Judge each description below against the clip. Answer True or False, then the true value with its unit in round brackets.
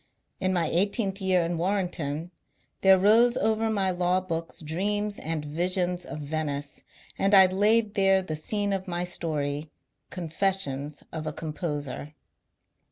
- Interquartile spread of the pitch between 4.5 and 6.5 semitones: False (3.8 semitones)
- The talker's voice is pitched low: False (180 Hz)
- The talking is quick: False (150 wpm)